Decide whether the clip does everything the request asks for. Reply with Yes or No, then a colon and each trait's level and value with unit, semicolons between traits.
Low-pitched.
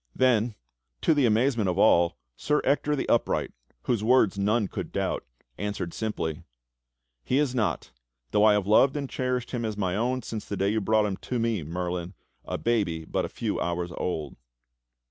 Yes: low, 110 Hz